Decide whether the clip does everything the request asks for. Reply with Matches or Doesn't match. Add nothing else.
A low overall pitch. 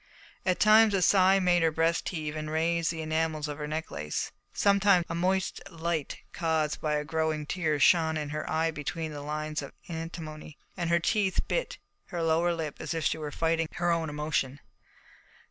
Doesn't match